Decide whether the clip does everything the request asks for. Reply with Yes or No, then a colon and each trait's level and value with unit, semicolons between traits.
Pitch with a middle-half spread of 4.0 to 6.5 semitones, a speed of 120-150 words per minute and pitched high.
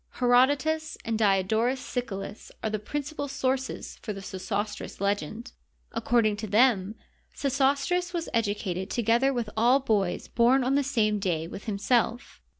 Yes: average, 4.4 semitones; average, 140 wpm; high, 230 Hz